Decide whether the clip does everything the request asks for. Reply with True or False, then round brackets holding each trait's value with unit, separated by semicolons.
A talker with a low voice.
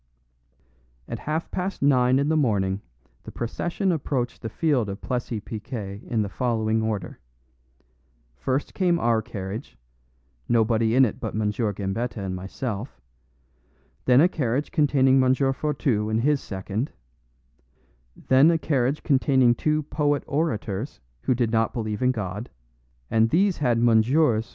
True (120 Hz)